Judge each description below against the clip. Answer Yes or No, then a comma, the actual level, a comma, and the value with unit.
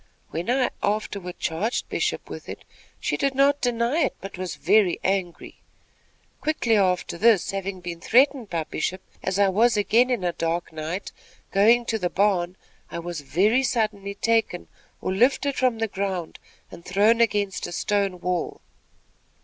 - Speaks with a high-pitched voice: Yes, high, 200 Hz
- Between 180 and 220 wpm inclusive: No, average, 160 wpm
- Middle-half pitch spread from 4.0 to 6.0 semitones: Yes, average, 4.4 semitones